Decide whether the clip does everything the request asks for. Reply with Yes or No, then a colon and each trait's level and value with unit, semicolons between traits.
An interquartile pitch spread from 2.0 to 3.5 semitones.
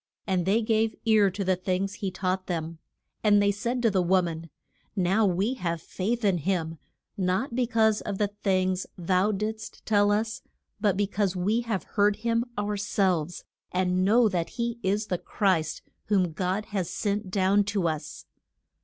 Yes: narrow, 2.6 semitones